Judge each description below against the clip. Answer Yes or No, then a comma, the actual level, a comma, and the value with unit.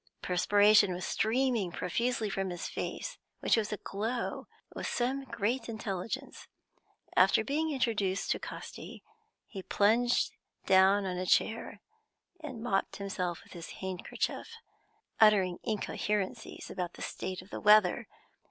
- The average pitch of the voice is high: Yes, high, 205 Hz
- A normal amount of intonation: Yes, average, 3.6 semitones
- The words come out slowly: Yes, slow, 125 wpm